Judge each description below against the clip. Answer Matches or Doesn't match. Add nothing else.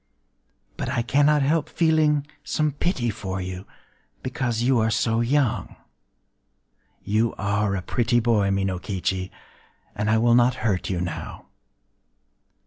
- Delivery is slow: Matches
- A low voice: Matches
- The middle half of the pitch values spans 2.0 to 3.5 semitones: Doesn't match